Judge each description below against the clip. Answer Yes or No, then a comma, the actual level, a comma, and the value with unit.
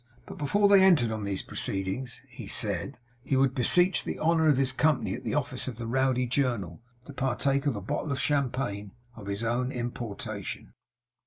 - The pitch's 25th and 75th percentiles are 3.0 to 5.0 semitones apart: Yes, average, 3.7 semitones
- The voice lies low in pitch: Yes, low, 130 Hz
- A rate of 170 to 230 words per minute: Yes, average, 185 wpm